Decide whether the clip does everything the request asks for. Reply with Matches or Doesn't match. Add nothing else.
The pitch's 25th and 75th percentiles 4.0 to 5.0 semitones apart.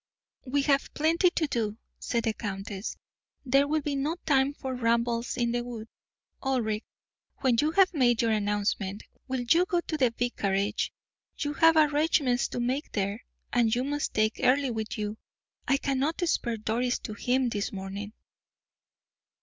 Matches